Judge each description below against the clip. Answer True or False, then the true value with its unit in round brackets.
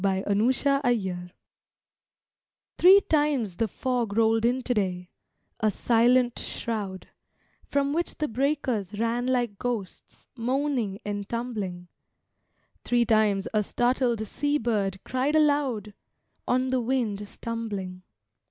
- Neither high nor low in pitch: False (230 Hz)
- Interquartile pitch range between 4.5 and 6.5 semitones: False (4.0 semitones)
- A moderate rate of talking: False (105 wpm)